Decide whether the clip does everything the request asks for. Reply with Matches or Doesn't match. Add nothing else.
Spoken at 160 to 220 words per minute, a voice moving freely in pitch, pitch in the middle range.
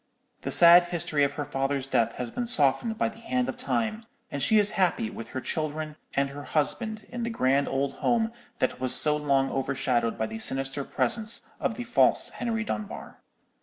Matches